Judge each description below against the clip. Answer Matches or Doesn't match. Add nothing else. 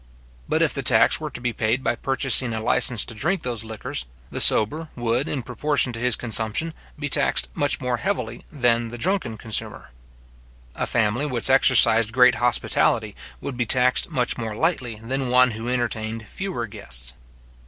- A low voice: Matches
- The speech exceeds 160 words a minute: Matches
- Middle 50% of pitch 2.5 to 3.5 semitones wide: Matches